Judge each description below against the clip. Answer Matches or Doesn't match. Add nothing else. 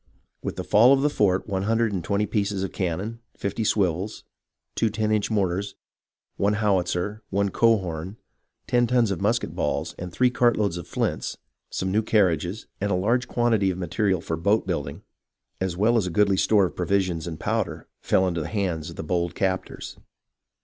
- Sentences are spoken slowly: Doesn't match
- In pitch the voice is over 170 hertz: Doesn't match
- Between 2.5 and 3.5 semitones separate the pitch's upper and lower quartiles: Matches